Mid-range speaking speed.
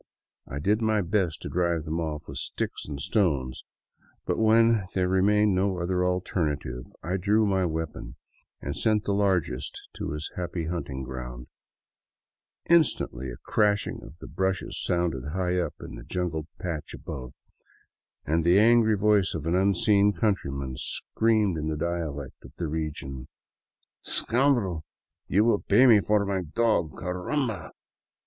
Yes: average, 150 wpm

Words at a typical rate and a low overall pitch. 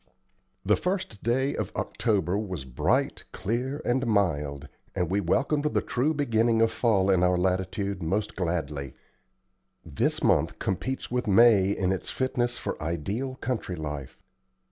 Yes: average, 145 wpm; low, 100 Hz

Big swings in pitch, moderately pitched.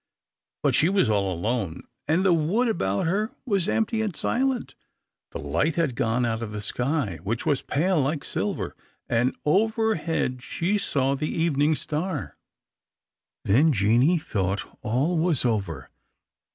Yes: wide, 7.8 semitones; medium, 150 Hz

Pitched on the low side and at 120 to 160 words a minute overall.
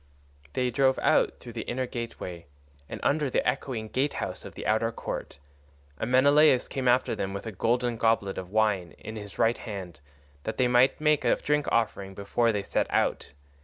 No: low, 115 Hz; average, 185 wpm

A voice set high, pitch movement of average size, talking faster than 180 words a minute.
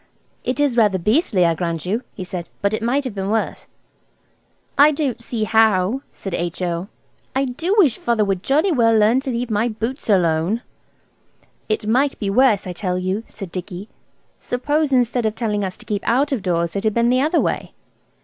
Yes: high, 220 Hz; average, 5.0 semitones; average, 190 wpm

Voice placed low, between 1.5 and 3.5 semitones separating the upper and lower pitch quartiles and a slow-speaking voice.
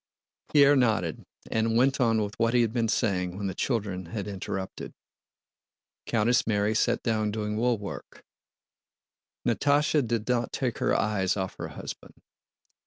No: low, 110 Hz; average, 2.9 semitones; average, 145 wpm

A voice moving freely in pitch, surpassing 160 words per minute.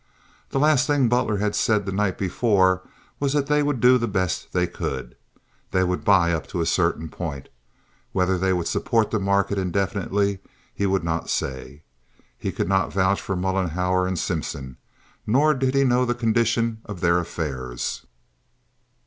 No: average, 4.6 semitones; average, 170 wpm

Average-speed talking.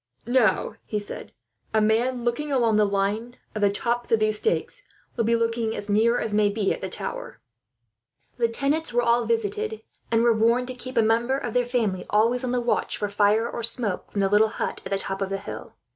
No: fast, 220 wpm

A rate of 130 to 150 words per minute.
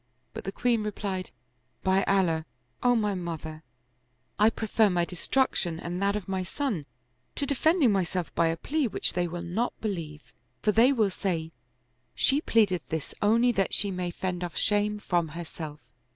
No: average, 175 wpm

